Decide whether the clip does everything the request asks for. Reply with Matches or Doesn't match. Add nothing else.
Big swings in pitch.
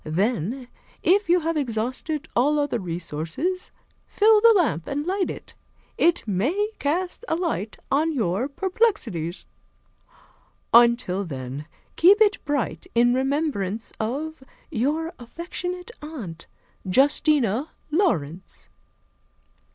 Matches